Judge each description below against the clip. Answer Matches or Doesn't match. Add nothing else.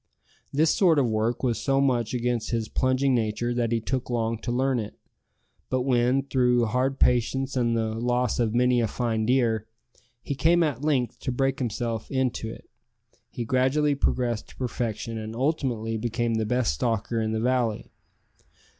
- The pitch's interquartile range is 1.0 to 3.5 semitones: Matches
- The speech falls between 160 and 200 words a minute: Matches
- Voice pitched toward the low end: Matches